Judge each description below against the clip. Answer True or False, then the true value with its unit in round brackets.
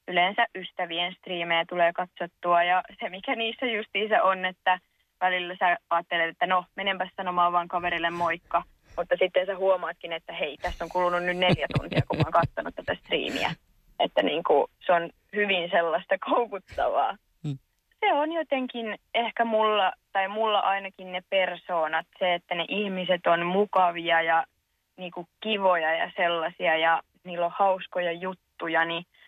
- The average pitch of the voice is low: False (180 Hz)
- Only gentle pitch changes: True (2.3 semitones)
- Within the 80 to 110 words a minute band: False (150 wpm)